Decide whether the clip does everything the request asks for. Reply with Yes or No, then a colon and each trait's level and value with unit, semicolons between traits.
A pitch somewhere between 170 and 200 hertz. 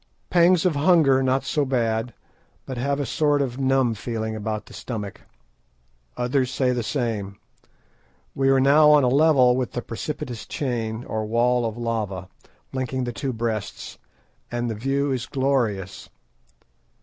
No: low, 125 Hz